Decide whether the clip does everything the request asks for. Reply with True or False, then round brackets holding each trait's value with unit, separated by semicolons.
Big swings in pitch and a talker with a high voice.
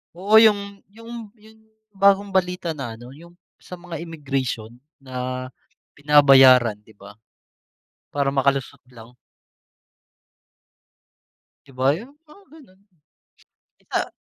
False (7.5 semitones; 150 Hz)